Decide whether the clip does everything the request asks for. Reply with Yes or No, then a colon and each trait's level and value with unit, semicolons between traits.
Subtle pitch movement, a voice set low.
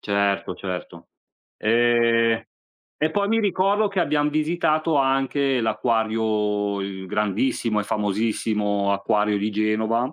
No: average, 5.1 semitones; low, 110 Hz